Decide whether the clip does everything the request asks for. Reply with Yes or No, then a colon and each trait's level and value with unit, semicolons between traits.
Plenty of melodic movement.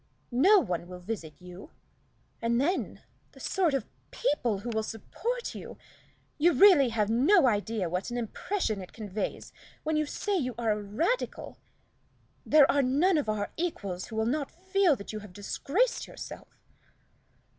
Yes: wide, 7.7 semitones